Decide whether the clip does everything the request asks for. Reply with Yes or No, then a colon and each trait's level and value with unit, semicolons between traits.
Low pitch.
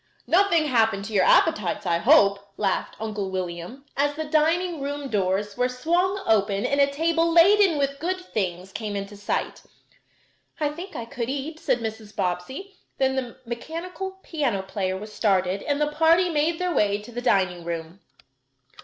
No: very high, 250 Hz